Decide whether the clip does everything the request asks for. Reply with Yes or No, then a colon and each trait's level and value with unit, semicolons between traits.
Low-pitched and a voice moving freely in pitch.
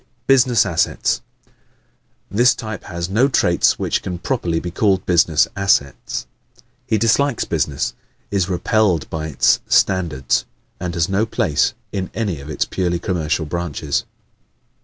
No: very low, 90 Hz; average, 4.6 semitones